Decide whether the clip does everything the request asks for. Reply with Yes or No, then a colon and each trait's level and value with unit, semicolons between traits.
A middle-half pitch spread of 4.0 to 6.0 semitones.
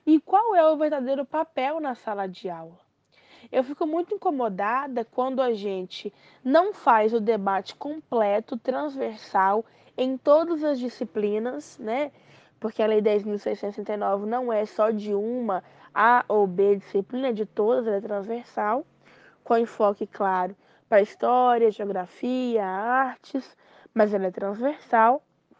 Yes: average, 4.3 semitones